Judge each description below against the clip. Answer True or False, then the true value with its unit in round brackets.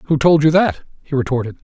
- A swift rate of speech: True (210 wpm)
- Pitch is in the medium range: True (150 Hz)